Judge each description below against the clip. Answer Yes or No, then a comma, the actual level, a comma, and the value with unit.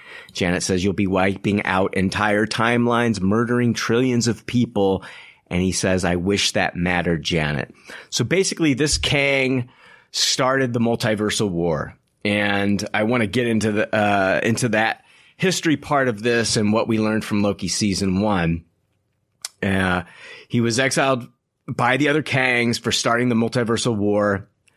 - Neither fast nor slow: Yes, average, 155 wpm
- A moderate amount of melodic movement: Yes, average, 3.5 semitones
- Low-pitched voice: Yes, low, 110 Hz